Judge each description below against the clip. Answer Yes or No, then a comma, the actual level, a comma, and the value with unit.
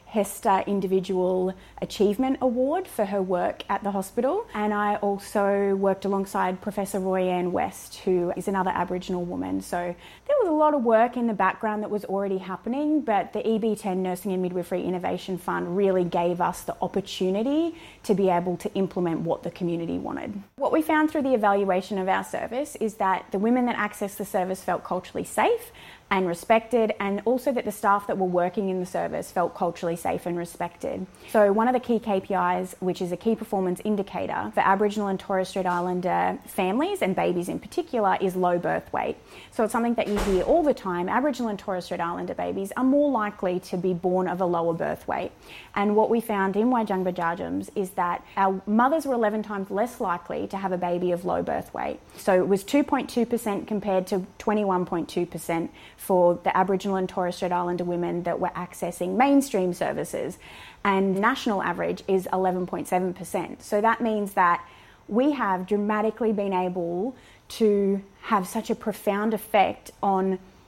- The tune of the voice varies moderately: Yes, average, 3.0 semitones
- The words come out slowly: No, average, 185 wpm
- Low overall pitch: No, high, 195 Hz